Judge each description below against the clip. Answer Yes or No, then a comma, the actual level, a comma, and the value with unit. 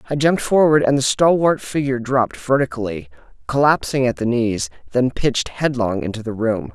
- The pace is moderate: Yes, average, 160 wpm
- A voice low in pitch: Yes, low, 125 Hz